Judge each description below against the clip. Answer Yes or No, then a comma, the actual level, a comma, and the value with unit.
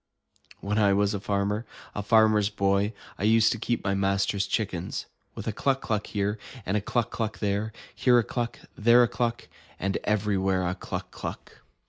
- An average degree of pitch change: No, narrow, 2.1 semitones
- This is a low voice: Yes, low, 105 Hz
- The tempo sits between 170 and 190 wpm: Yes, average, 185 wpm